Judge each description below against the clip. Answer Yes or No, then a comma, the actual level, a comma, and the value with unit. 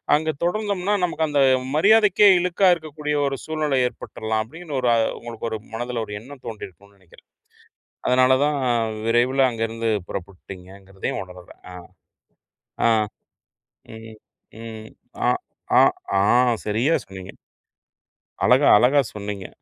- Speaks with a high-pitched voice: No, low, 120 Hz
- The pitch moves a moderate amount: No, wide, 6.3 semitones